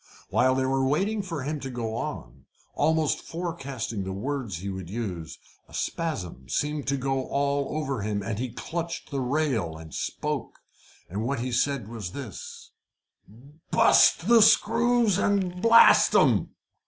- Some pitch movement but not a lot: No, wide, 6.6 semitones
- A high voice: No, low, 135 Hz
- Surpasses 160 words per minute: No, average, 155 wpm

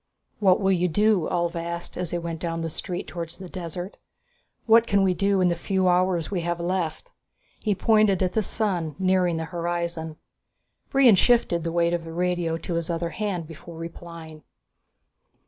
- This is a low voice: No, medium, 175 Hz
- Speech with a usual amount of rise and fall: No, narrow, 2.1 semitones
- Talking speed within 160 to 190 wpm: Yes, average, 180 wpm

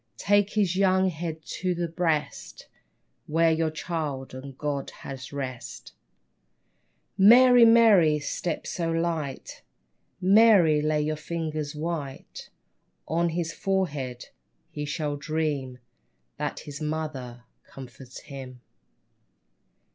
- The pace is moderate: No, slow, 105 wpm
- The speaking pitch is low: No, medium, 155 Hz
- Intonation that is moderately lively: Yes, average, 3.5 semitones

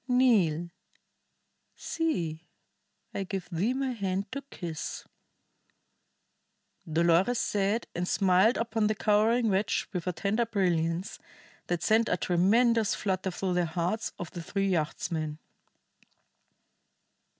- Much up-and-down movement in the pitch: No, average, 4.3 semitones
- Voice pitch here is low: No, high, 195 Hz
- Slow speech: Yes, slow, 115 wpm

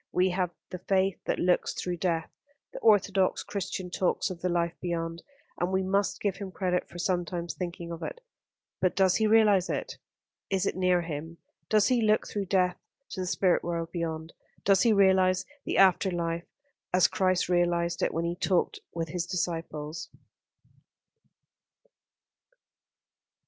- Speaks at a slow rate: No, average, 160 wpm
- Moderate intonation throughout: No, narrow, 2.0 semitones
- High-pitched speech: No, medium, 180 Hz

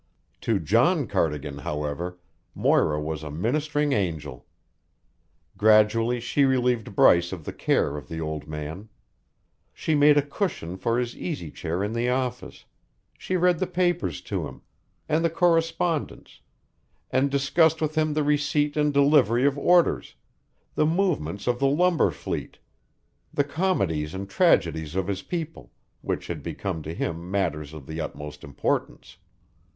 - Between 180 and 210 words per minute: No, average, 145 wpm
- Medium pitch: No, low, 115 Hz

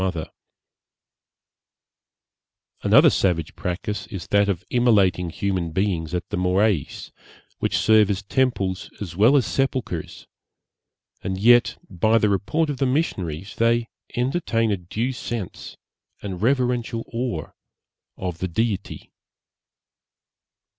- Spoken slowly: Yes, slow, 115 wpm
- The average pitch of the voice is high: No, low, 100 Hz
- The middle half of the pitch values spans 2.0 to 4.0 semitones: No, average, 4.6 semitones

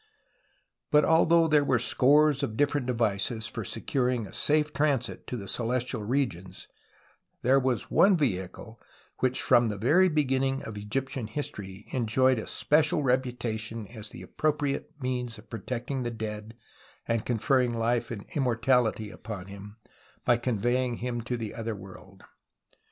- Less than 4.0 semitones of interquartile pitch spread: Yes, average, 3.4 semitones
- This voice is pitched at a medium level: No, low, 120 Hz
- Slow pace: No, average, 145 wpm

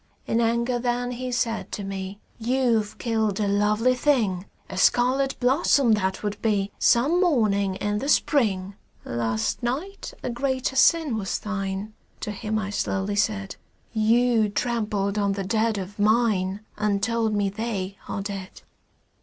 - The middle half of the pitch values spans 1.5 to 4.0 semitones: Yes, average, 3.3 semitones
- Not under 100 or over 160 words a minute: Yes, average, 150 wpm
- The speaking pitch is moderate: No, high, 215 Hz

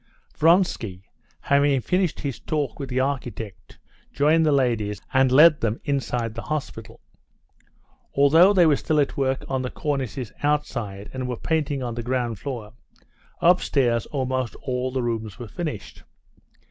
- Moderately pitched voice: No, low, 130 Hz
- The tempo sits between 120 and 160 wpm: Yes, average, 145 wpm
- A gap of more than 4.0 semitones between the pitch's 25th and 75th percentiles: No, average, 3.7 semitones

